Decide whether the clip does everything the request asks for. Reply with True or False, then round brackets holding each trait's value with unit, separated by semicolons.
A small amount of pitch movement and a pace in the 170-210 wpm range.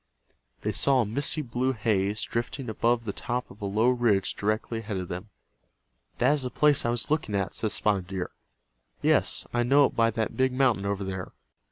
False (3.8 semitones; 200 wpm)